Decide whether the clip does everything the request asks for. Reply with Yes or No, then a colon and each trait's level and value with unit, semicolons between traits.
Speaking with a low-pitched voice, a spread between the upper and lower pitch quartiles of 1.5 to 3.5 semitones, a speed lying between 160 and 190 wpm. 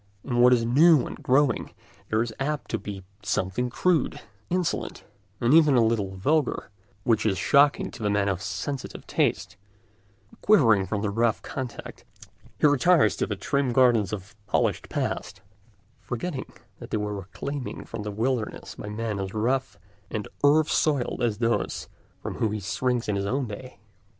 No: low, 120 Hz; average, 4.8 semitones; average, 165 wpm